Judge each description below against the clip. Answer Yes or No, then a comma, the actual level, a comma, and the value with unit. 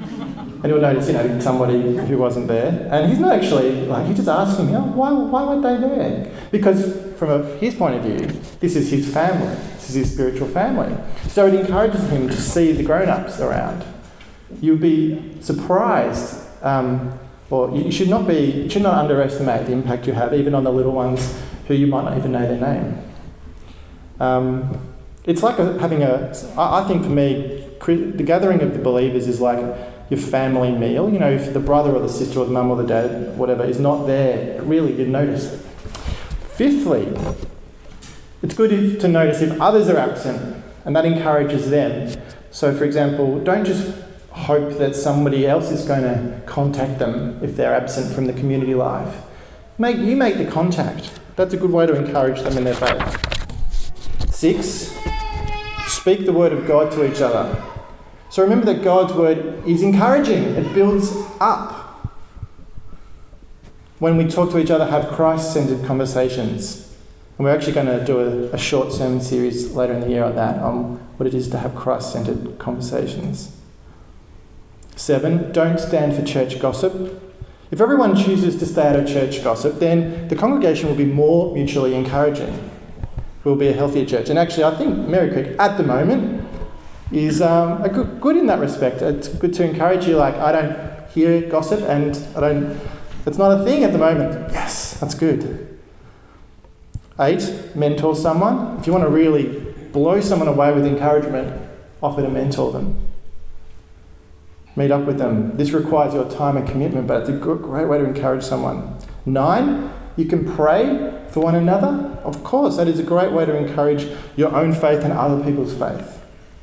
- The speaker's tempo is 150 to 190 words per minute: Yes, average, 180 wpm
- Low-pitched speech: No, medium, 145 Hz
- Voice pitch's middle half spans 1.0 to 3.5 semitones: No, average, 4.7 semitones